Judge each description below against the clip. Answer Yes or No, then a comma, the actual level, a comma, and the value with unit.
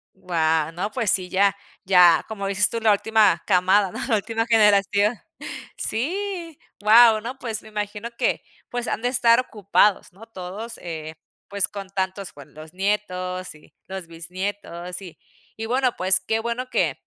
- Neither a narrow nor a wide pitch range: Yes, average, 3.6 semitones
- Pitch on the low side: No, high, 200 Hz